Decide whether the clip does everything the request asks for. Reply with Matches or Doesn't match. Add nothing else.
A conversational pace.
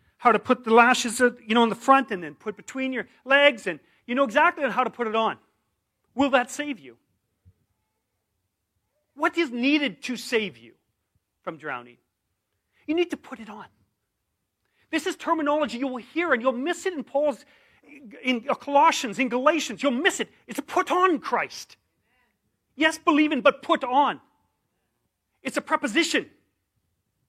Matches